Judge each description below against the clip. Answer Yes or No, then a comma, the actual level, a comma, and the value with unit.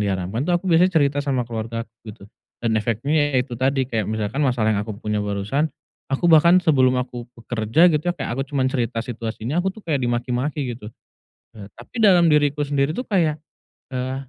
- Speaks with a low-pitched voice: Yes, low, 130 Hz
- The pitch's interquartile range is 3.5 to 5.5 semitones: Yes, average, 4.7 semitones